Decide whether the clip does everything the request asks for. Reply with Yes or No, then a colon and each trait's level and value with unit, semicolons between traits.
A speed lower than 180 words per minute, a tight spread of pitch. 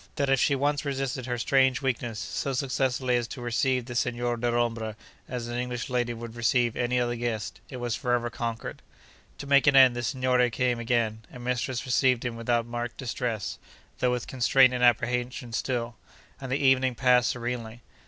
No: average, 185 wpm; narrow, 1.4 semitones